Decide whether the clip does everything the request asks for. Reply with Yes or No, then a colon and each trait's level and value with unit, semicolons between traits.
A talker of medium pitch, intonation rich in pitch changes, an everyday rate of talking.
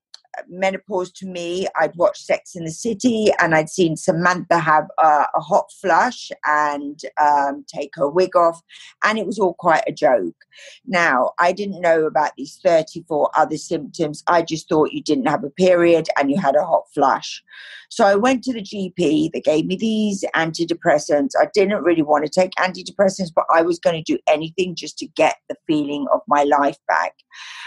No: medium, 175 Hz; average, 4.3 semitones; average, 190 wpm